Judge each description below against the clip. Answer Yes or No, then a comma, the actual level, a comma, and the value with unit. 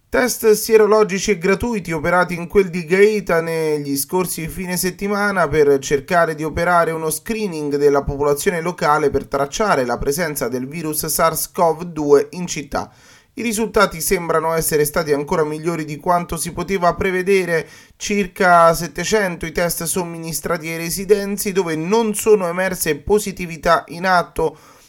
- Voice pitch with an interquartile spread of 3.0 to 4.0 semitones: Yes, average, 3.6 semitones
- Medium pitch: Yes, medium, 175 Hz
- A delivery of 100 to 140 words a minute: Yes, average, 135 wpm